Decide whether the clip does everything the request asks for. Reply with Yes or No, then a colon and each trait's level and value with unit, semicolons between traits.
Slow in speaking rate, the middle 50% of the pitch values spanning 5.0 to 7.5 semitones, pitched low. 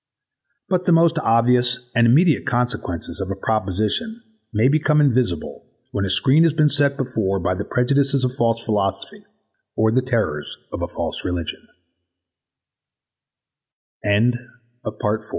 Yes: slow, 130 wpm; wide, 5.4 semitones; low, 125 Hz